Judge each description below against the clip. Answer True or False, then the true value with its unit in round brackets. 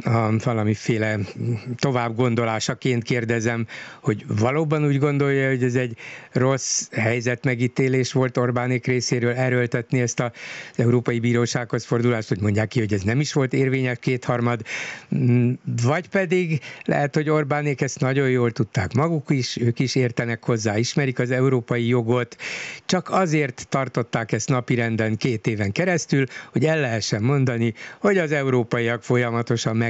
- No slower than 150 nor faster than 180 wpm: False (140 wpm)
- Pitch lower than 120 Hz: False (125 Hz)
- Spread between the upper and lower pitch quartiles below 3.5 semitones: True (2.6 semitones)